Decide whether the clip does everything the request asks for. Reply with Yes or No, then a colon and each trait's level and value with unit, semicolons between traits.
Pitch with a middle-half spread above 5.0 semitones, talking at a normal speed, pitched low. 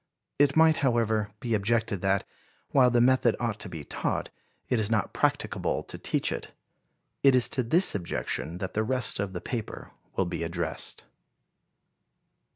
No: average, 4.5 semitones; average, 160 wpm; low, 110 Hz